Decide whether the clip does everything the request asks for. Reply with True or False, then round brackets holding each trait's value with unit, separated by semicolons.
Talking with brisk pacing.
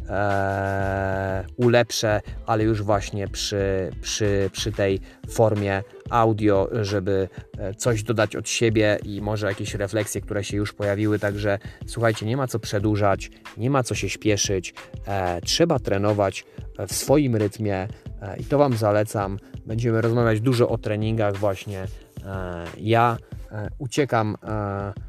False (135 wpm)